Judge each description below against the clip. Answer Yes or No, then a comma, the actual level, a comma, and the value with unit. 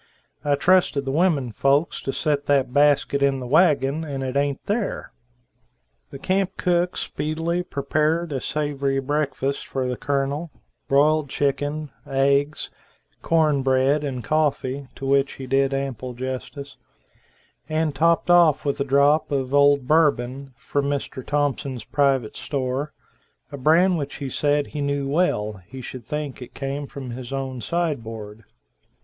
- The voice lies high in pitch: No, medium, 140 Hz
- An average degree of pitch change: No, narrow, 2.1 semitones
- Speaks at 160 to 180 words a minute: No, average, 150 wpm